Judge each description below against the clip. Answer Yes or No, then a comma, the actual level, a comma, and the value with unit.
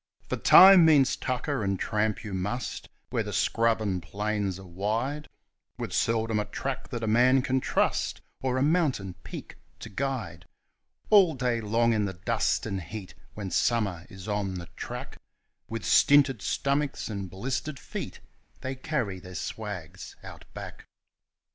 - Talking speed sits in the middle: Yes, average, 155 wpm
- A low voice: Yes, low, 110 Hz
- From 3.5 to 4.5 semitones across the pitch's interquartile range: No, average, 5.1 semitones